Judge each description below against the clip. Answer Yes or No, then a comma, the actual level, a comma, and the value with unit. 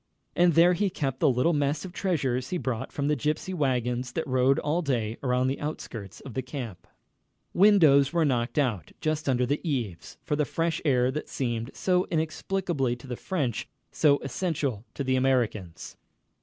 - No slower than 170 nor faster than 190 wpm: Yes, average, 180 wpm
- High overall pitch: No, medium, 140 Hz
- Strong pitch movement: No, average, 4.2 semitones